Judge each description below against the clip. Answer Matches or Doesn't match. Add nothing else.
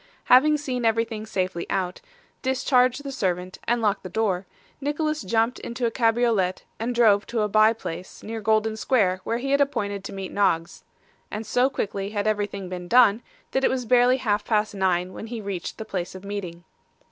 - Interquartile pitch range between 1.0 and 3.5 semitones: Doesn't match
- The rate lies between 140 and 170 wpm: Doesn't match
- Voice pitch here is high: Matches